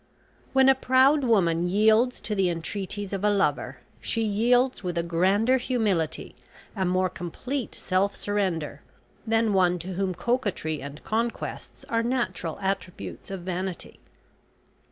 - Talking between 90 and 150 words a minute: Yes, slow, 135 wpm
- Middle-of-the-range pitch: No, high, 195 Hz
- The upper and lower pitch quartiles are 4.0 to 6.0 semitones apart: Yes, average, 4.4 semitones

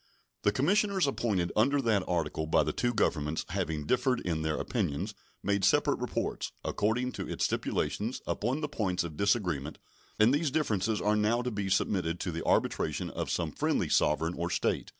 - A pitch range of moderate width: No, wide, 6.1 semitones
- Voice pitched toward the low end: Yes, low, 105 Hz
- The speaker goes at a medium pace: Yes, average, 175 wpm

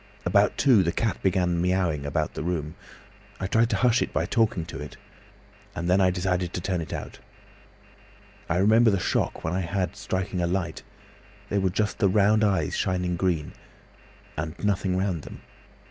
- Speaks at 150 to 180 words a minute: Yes, average, 175 wpm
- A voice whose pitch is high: No, very low, 90 Hz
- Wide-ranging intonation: No, narrow, 2.6 semitones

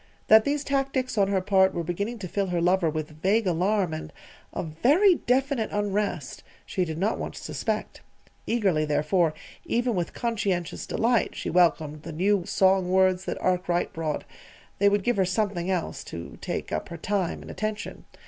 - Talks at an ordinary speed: Yes, average, 175 wpm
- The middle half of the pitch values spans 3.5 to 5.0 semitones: Yes, average, 4.0 semitones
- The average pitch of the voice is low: No, high, 190 Hz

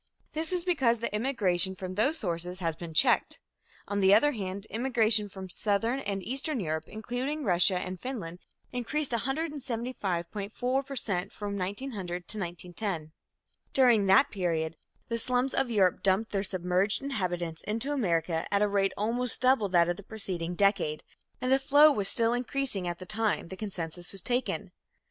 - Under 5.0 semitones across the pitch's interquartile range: No, wide, 5.5 semitones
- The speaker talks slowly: No, average, 165 wpm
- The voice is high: Yes, high, 205 Hz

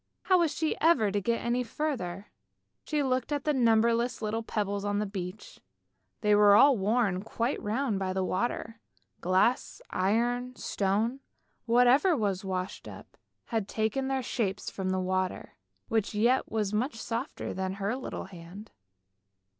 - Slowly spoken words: No, average, 155 wpm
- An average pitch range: Yes, average, 4.2 semitones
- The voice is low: No, high, 220 Hz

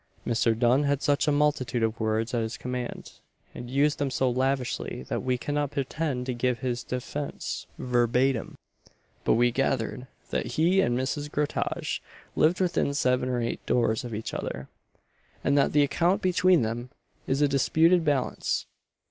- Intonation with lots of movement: No, average, 3.2 semitones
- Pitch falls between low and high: No, low, 130 Hz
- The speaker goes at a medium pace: Yes, average, 165 wpm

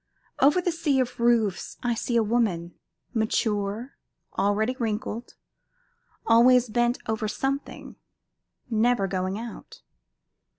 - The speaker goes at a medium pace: No, slow, 110 wpm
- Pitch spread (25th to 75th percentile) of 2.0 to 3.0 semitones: Yes, average, 2.7 semitones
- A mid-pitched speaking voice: No, high, 230 Hz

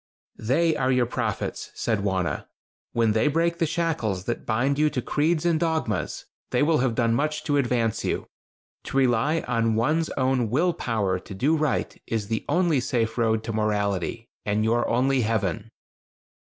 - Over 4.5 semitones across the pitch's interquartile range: Yes, wide, 5.4 semitones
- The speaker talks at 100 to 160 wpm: No, average, 170 wpm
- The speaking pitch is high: No, low, 120 Hz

